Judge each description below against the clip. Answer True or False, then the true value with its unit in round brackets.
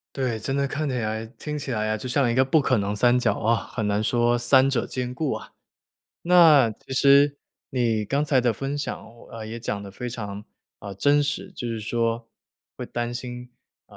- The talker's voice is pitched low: True (120 Hz)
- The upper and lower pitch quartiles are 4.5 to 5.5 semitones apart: False (4.0 semitones)